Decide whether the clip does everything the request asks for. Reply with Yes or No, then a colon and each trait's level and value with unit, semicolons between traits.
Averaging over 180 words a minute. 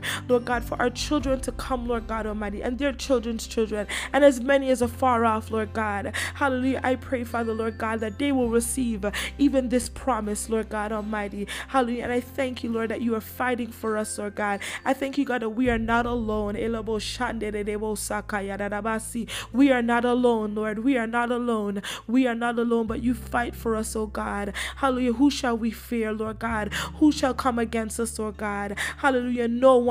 Yes: average, 200 wpm